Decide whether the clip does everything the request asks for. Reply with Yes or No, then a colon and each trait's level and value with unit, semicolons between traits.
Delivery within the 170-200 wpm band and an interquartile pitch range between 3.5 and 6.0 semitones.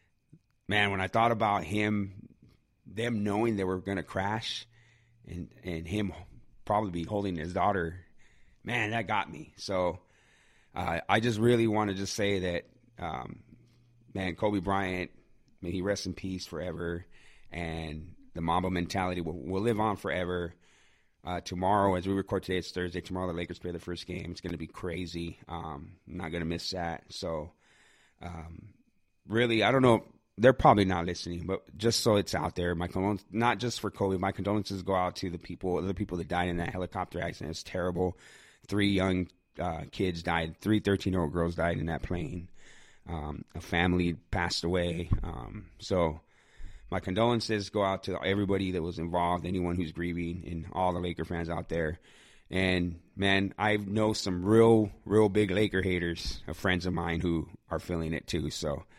No: average, 185 wpm; average, 2.9 semitones